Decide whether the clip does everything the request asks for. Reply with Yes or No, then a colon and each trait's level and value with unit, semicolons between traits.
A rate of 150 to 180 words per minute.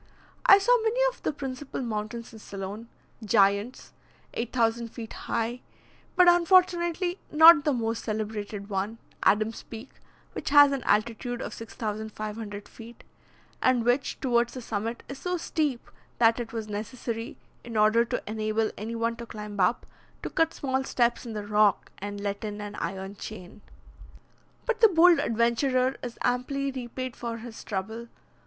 Yes: average, 155 wpm